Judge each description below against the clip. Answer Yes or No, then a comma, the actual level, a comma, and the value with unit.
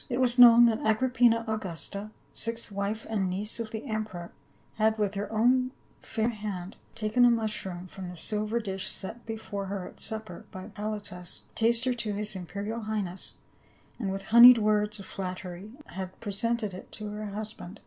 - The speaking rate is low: No, average, 170 wpm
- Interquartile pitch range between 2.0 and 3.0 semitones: Yes, average, 2.7 semitones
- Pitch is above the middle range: Yes, high, 215 Hz